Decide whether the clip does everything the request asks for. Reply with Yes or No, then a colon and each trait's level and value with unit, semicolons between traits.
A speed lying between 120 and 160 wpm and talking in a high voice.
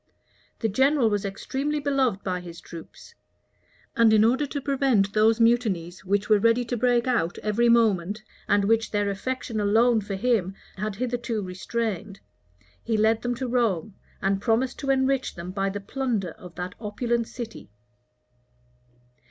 Yes: average, 155 wpm; high, 220 Hz